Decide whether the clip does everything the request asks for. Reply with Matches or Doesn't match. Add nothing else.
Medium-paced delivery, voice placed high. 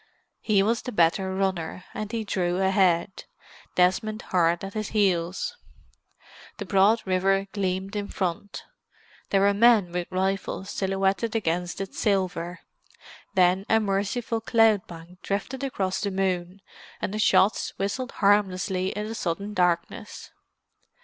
Doesn't match